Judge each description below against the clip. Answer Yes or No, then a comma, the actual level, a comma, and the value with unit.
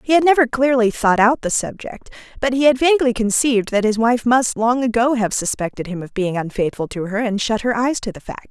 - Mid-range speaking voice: No, high, 230 Hz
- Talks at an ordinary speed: No, fast, 240 wpm